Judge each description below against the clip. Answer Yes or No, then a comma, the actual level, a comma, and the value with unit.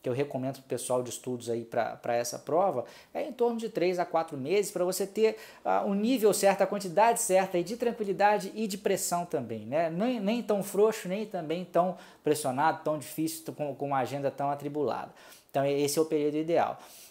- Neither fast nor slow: No, fast, 215 wpm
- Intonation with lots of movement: Yes, wide, 6.3 semitones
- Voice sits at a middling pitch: Yes, medium, 175 Hz